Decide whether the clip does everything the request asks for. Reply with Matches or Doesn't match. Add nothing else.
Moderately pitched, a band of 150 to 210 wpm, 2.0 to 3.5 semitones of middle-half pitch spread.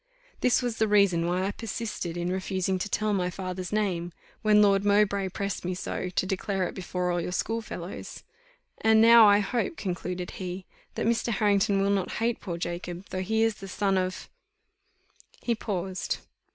Doesn't match